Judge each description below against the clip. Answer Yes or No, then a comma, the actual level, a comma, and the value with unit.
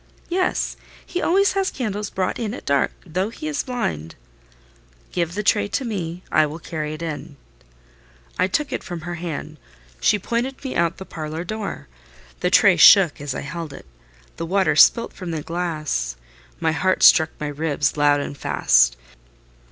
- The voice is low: No, medium, 170 Hz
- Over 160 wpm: Yes, average, 175 wpm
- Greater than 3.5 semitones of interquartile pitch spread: Yes, wide, 5.4 semitones